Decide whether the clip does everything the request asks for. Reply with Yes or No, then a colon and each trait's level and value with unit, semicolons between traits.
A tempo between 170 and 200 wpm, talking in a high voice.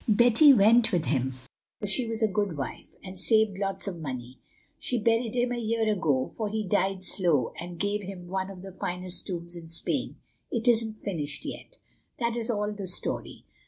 Yes: average, 190 wpm; high, 195 Hz